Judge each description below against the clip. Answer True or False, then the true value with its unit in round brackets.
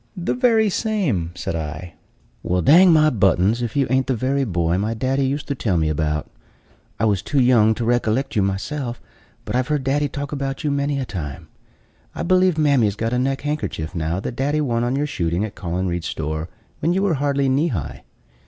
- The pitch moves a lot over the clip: True (7.3 semitones)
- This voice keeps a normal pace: False (210 wpm)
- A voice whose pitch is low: True (125 Hz)